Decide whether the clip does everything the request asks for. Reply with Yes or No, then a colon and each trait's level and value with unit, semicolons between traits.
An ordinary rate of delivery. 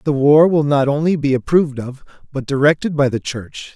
No: fast, 210 wpm